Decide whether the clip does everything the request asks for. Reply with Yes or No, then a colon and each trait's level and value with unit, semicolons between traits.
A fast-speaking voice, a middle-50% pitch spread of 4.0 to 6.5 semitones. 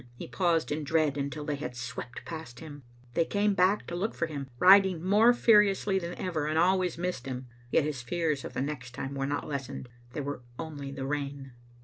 Yes: fast, 210 wpm; average, 4.6 semitones